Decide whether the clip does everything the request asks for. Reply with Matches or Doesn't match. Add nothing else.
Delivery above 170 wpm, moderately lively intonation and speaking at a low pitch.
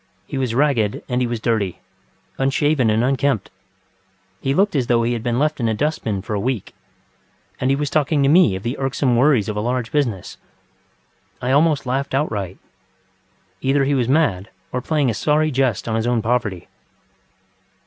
Matches